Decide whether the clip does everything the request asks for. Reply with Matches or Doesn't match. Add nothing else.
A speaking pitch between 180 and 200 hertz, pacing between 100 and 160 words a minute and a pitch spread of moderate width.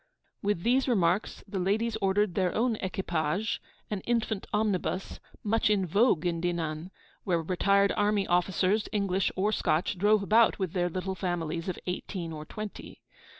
Matches